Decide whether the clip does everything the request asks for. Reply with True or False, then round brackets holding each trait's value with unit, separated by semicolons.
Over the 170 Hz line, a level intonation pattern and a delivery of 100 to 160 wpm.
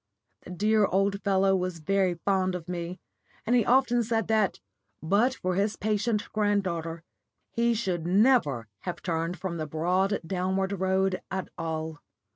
False (190 Hz; 3.0 semitones; 150 wpm)